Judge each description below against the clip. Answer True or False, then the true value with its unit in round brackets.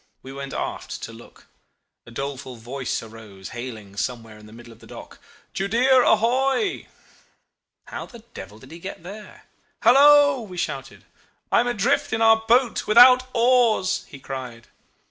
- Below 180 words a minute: True (155 wpm)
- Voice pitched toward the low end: False (185 Hz)